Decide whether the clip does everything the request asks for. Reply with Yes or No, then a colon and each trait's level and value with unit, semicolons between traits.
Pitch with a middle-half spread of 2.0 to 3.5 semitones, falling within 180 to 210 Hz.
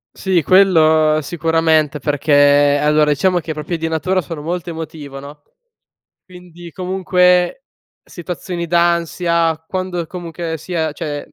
No: narrow, 2.6 semitones; medium, 165 Hz